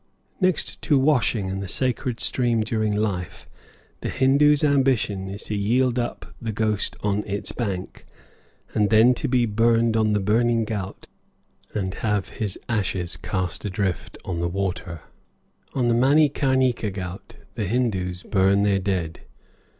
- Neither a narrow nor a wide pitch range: Yes, average, 4.0 semitones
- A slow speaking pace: No, average, 145 wpm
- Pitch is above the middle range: No, low, 110 Hz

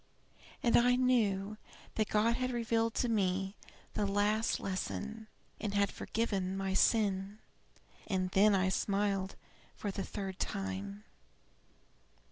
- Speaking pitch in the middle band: No, high, 200 Hz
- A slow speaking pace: Yes, slow, 120 wpm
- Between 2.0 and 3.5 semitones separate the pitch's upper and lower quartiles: Yes, narrow, 2.6 semitones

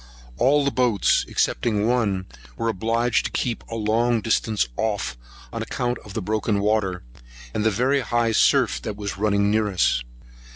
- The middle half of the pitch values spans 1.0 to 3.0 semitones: Yes, narrow, 2.6 semitones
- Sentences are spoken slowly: No, average, 165 wpm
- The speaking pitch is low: Yes, low, 110 Hz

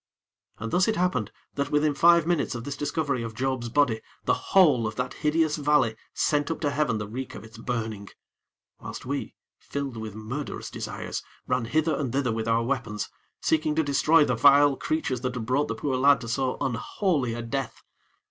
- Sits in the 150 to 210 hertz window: No, low, 135 Hz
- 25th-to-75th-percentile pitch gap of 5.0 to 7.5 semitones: No, average, 4.3 semitones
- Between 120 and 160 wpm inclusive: No, average, 195 wpm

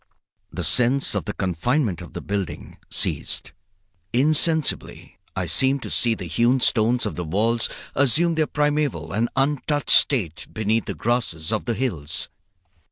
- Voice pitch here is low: Yes, low, 120 Hz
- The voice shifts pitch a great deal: Yes, wide, 5.7 semitones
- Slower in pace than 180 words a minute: Yes, average, 150 wpm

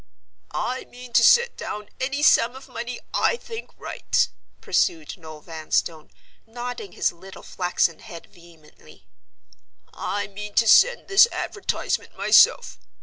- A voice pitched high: Yes, high, 225 Hz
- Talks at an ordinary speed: No, slow, 130 wpm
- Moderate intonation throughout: No, wide, 8.1 semitones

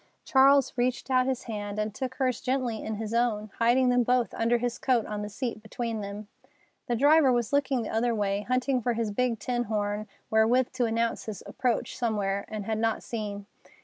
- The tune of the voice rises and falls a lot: No, average, 2.9 semitones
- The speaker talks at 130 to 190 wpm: No, average, 200 wpm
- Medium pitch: No, high, 230 Hz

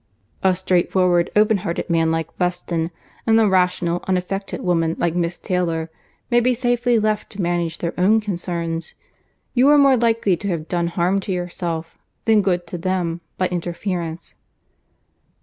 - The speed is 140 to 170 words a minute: Yes, average, 155 wpm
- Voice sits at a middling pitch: Yes, medium, 180 Hz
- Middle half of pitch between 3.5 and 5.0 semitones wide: No, average, 3.1 semitones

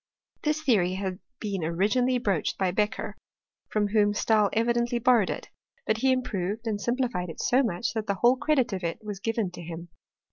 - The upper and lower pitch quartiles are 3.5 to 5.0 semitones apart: Yes, average, 4.1 semitones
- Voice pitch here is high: Yes, high, 215 Hz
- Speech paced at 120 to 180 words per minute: No, average, 190 wpm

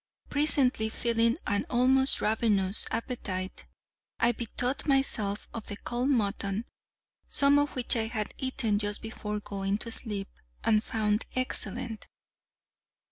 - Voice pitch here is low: No, high, 225 Hz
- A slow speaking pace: Yes, slow, 125 wpm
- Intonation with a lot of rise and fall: No, average, 3.3 semitones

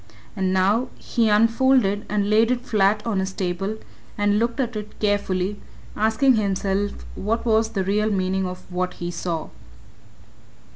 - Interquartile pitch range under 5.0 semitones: Yes, average, 2.7 semitones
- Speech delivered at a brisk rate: No, average, 150 wpm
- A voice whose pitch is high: Yes, high, 205 Hz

